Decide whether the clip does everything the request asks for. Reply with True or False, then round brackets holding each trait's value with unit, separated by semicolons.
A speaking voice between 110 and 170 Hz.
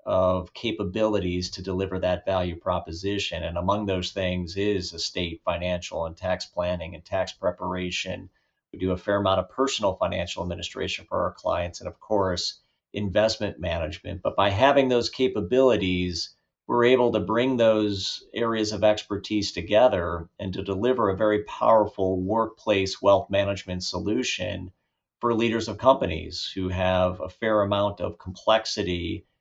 False (100 Hz)